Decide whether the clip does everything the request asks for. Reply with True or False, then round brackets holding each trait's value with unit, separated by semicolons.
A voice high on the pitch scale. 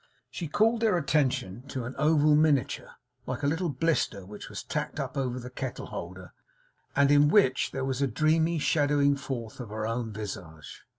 False (140 Hz)